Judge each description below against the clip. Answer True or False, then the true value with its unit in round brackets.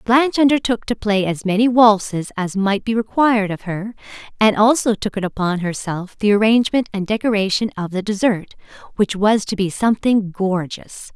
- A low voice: False (210 Hz)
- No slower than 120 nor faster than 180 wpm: True (165 wpm)